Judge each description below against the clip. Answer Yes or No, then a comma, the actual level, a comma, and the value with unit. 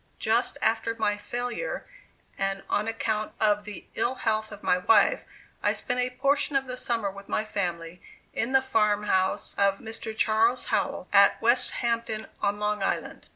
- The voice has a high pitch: Yes, high, 215 Hz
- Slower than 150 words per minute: No, average, 160 wpm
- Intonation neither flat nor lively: Yes, average, 3.0 semitones